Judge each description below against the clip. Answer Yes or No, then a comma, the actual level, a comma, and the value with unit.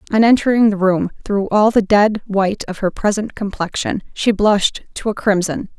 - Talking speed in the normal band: Yes, average, 185 wpm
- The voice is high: Yes, high, 205 Hz